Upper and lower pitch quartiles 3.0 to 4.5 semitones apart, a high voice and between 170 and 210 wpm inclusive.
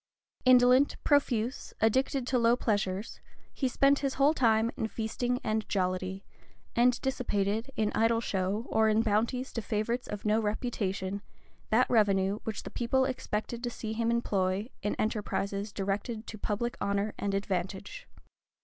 No: average, 3.3 semitones; high, 220 Hz; average, 150 wpm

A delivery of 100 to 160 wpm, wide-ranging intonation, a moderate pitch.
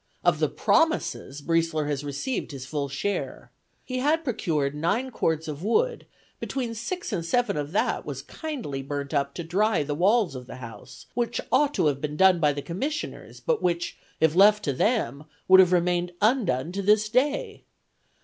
No: average, 180 wpm; wide, 8.3 semitones; medium, 175 Hz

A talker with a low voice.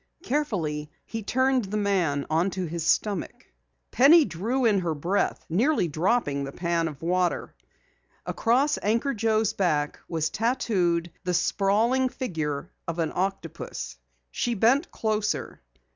No: high, 195 Hz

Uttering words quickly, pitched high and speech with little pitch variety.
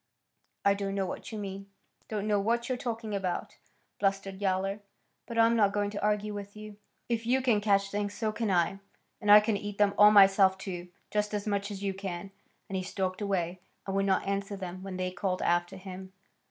Yes: fast, 210 wpm; high, 200 Hz; narrow, 1.5 semitones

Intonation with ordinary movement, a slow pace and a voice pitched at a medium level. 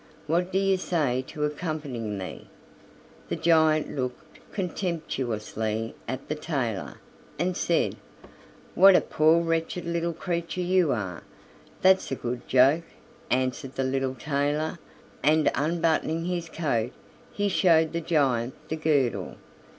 Yes: average, 4.6 semitones; slow, 125 wpm; medium, 155 Hz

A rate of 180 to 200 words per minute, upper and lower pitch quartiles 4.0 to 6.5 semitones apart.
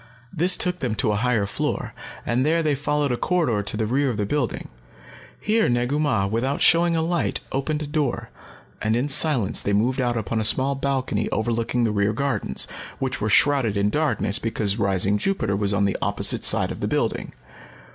Yes: average, 195 wpm; wide, 5.6 semitones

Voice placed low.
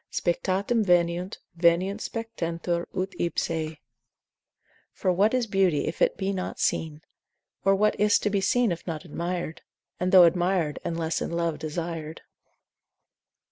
No: medium, 175 Hz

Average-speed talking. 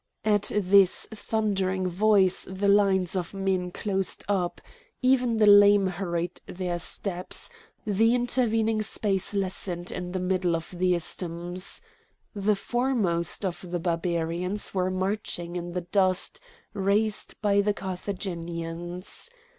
No: slow, 125 wpm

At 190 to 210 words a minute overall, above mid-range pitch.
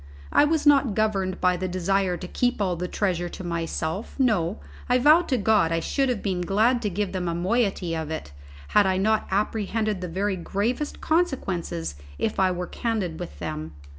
Yes: average, 195 wpm; high, 195 Hz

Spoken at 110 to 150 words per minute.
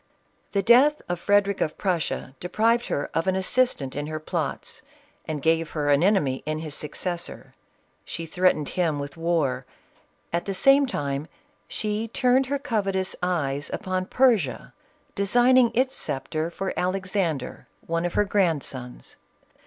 Yes: average, 145 wpm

